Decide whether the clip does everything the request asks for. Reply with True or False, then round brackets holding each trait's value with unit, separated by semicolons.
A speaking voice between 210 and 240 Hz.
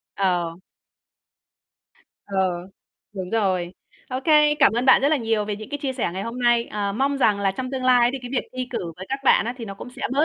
True (230 Hz)